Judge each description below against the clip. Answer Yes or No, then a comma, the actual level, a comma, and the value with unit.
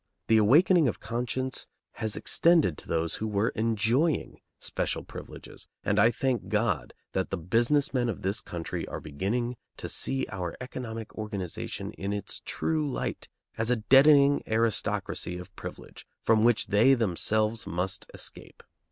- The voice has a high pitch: No, low, 115 Hz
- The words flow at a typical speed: Yes, average, 150 wpm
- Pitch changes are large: No, average, 4.2 semitones